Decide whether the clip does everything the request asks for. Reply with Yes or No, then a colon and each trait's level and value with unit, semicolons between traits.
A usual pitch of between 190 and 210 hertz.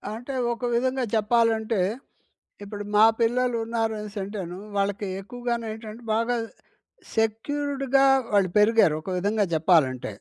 No: high, 225 Hz